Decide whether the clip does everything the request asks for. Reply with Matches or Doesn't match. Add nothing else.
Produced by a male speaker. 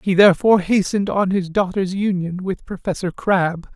Matches